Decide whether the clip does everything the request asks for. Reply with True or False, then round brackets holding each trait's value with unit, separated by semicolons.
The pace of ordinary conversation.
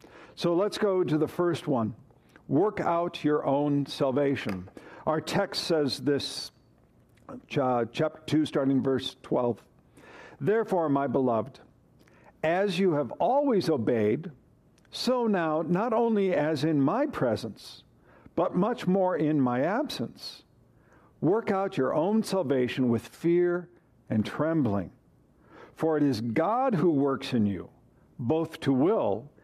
False (130 wpm)